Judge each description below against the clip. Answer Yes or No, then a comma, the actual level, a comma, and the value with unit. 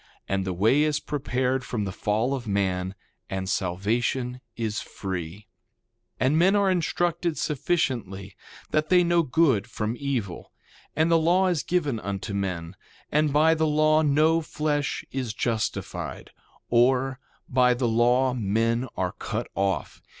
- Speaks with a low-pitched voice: Yes, low, 125 Hz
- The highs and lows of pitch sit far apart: Yes, wide, 7.0 semitones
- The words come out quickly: No, average, 145 wpm